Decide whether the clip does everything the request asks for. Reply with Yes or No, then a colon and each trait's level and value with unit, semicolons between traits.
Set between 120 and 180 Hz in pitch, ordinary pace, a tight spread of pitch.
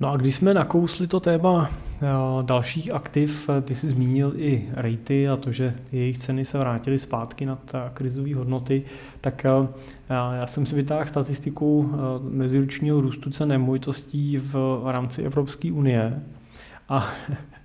Yes: low, 135 Hz; average, 135 wpm; narrow, 1.9 semitones